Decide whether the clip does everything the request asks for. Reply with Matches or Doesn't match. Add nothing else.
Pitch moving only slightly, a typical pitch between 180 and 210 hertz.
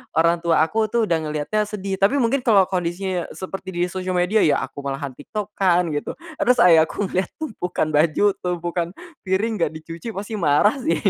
Doesn't match